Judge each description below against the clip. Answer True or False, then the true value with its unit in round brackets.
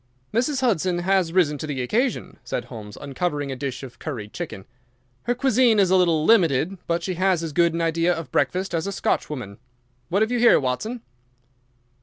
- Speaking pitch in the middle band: True (170 Hz)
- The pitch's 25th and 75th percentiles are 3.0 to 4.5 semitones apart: False (5.2 semitones)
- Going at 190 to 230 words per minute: True (195 wpm)